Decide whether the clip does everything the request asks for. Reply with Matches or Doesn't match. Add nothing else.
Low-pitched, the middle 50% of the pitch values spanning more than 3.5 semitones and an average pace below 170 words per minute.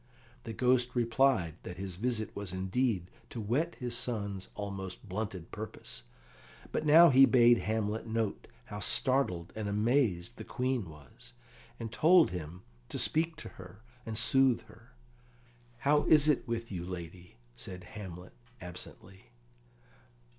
Matches